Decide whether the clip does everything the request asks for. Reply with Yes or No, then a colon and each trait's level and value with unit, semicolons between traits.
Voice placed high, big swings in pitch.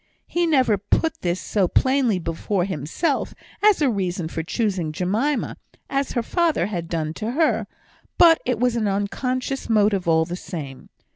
Yes: high, 210 Hz; wide, 7.2 semitones